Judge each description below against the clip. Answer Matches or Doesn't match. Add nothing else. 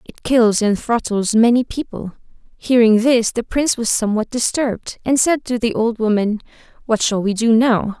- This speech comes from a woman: Matches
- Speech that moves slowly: Doesn't match